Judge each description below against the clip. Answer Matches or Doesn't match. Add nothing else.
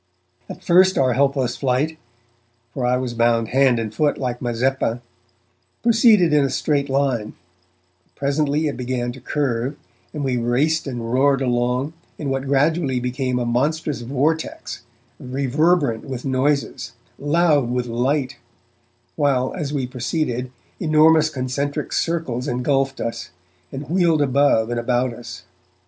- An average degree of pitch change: Matches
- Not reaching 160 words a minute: Matches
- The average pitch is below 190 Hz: Matches